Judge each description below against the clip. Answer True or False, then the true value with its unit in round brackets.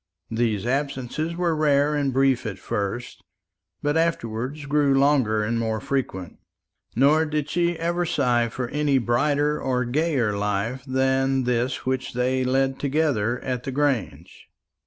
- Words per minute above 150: False (140 wpm)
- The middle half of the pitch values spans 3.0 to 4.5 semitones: True (3.6 semitones)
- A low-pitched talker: True (130 Hz)